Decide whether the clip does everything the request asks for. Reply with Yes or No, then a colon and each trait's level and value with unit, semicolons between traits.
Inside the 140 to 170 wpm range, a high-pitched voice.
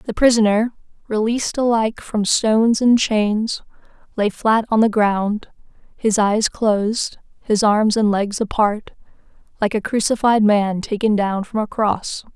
Yes: average, 145 wpm; high, 215 Hz